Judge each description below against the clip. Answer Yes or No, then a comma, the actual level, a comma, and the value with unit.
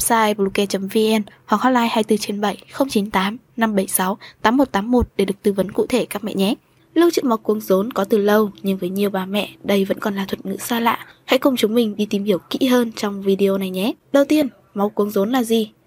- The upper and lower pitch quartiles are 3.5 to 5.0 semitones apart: No, average, 2.9 semitones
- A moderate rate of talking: Yes, average, 220 wpm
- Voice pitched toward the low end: No, high, 210 Hz